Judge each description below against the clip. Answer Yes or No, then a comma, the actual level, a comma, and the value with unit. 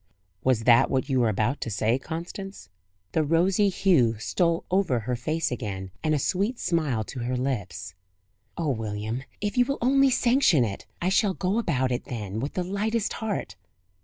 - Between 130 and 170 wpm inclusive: No, average, 180 wpm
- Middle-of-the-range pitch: Yes, medium, 145 Hz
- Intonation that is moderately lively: No, wide, 8.7 semitones